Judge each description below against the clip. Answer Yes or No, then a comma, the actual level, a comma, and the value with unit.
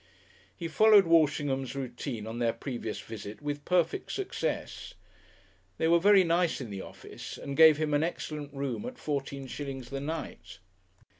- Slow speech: No, average, 155 wpm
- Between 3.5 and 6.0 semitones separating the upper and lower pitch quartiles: Yes, average, 3.8 semitones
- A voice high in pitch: No, medium, 145 Hz